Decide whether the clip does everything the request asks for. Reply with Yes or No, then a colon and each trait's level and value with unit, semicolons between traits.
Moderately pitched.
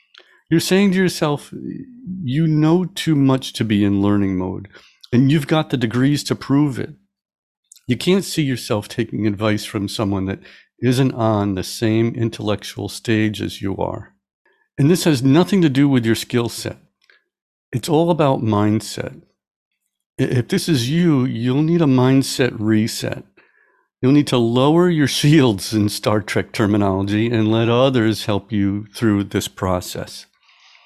No: low, 120 Hz